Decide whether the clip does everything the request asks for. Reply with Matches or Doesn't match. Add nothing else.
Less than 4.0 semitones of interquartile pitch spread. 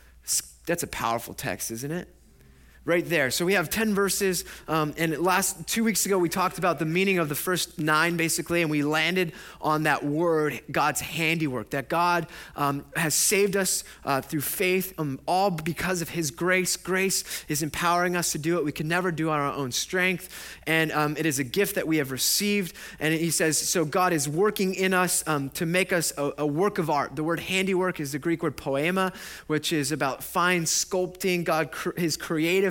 Matches